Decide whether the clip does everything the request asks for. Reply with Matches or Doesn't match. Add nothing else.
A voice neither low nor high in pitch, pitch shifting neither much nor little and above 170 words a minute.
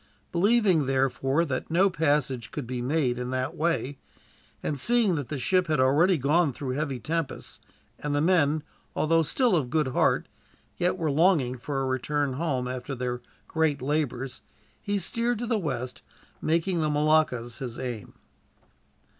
Doesn't match